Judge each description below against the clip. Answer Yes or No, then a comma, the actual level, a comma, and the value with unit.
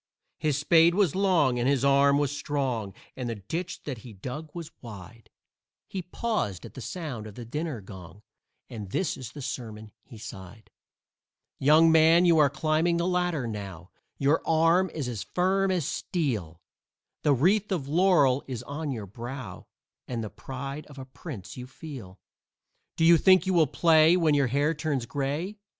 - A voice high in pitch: No, medium, 140 Hz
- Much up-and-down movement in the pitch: Yes, wide, 5.8 semitones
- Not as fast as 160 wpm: No, average, 175 wpm